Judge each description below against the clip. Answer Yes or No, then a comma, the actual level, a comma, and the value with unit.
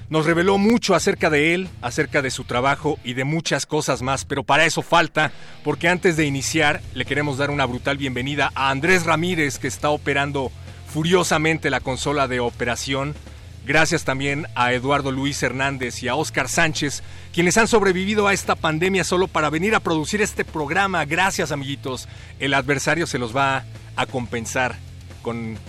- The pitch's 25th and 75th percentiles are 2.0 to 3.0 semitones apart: No, average, 4.2 semitones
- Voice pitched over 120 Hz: Yes, medium, 140 Hz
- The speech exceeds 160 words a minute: Yes, average, 170 wpm